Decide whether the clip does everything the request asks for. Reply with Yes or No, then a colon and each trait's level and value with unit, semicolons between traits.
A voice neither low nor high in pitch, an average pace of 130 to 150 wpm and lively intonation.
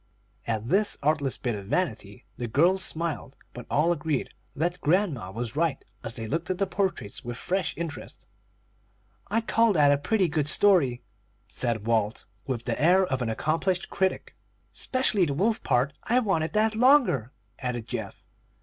No: medium, 155 Hz; average, 165 wpm; wide, 7.5 semitones